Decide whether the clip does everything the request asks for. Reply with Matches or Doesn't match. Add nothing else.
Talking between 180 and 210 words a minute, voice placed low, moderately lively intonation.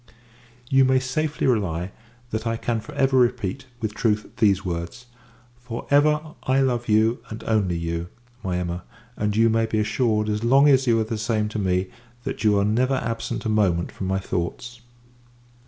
Matches